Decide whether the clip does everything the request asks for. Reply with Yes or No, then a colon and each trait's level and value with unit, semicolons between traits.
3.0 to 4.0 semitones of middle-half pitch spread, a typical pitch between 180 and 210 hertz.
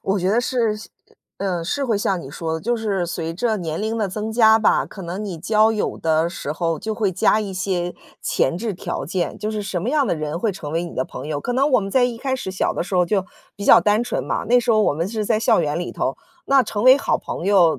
No: average, 4.4 semitones; high, 200 Hz